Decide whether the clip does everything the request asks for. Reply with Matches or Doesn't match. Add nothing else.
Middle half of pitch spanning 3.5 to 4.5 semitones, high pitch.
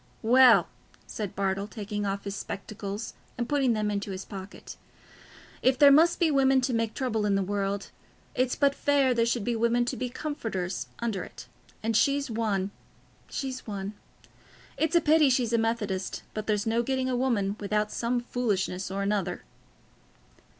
Matches